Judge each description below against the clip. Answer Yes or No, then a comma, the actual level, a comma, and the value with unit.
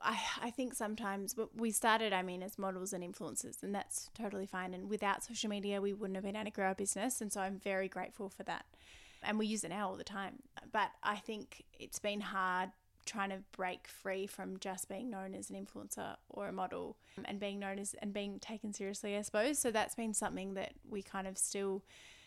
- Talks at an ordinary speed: No, fast, 225 wpm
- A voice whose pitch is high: Yes, high, 200 Hz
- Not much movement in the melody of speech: Yes, narrow, 2.0 semitones